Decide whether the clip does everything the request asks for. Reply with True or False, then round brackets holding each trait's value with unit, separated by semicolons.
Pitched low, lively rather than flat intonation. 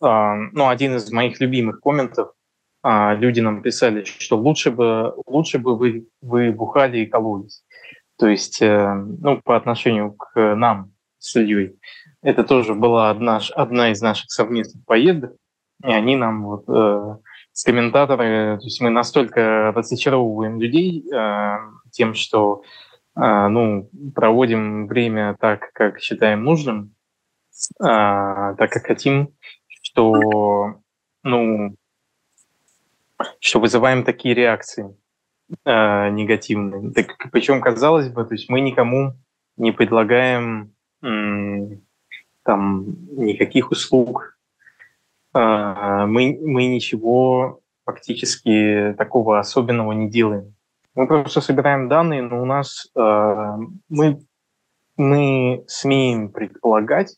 False (115 Hz; 3.4 semitones)